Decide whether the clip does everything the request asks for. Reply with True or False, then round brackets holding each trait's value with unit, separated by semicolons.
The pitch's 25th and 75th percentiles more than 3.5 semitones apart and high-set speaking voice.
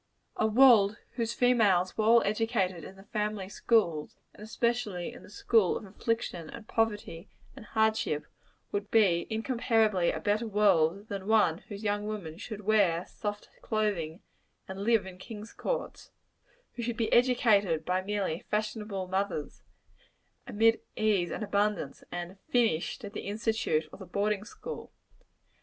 False (2.9 semitones; 210 Hz)